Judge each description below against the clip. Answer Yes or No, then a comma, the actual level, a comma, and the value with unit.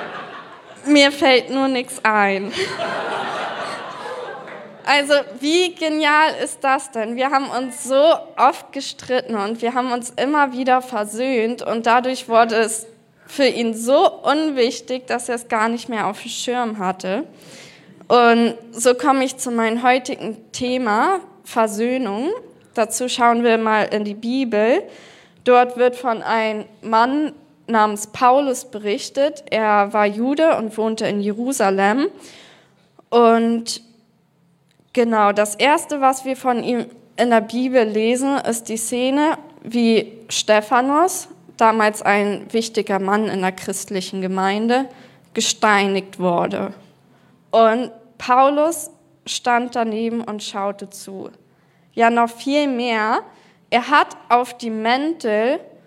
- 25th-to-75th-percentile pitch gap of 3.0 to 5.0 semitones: Yes, average, 3.5 semitones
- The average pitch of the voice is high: Yes, high, 235 Hz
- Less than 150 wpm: Yes, slow, 125 wpm